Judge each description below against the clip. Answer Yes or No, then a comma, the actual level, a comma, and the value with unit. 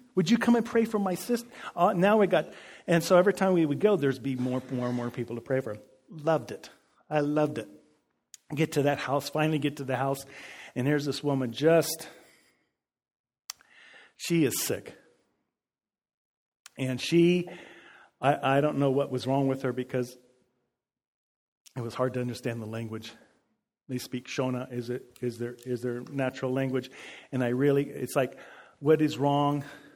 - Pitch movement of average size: Yes, average, 3.6 semitones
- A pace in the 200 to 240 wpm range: No, average, 180 wpm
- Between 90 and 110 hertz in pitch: No, low, 135 Hz